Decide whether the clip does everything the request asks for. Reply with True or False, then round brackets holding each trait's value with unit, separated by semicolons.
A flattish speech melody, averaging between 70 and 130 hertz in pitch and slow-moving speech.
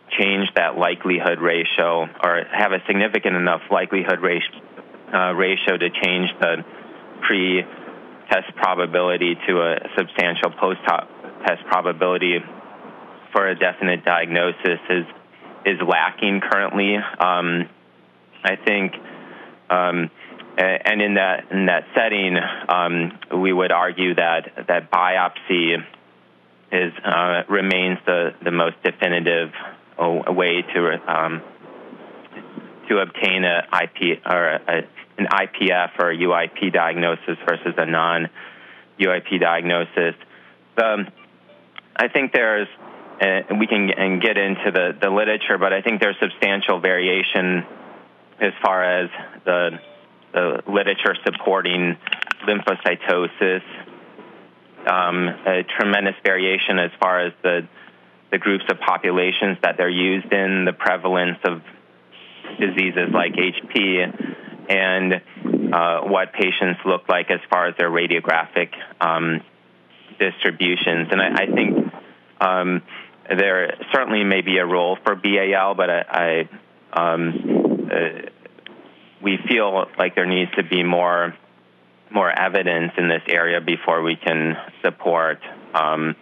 True (2.0 semitones; 90 Hz; 120 wpm)